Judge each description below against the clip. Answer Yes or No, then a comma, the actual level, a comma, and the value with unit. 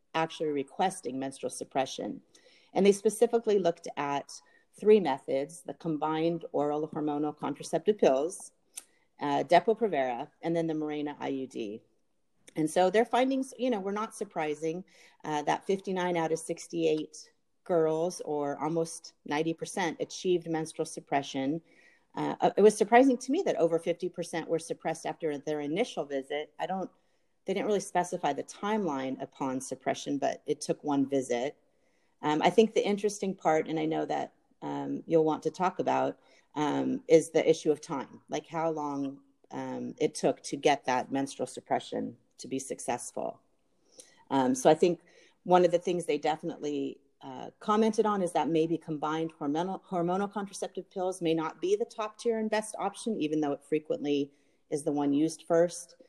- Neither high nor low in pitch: Yes, medium, 160 Hz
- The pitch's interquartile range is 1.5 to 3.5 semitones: No, average, 4.1 semitones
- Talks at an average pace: Yes, average, 165 wpm